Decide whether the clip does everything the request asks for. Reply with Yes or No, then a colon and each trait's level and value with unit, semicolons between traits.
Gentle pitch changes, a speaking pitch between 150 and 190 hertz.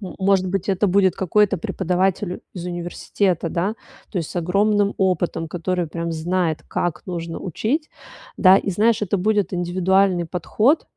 Yes: narrow, 2.3 semitones; medium, 185 Hz